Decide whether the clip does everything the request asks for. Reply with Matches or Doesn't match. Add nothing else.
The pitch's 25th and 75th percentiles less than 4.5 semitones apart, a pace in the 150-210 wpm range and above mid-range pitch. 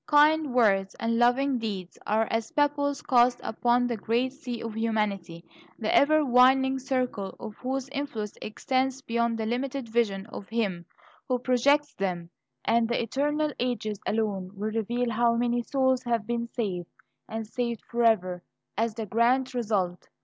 Matches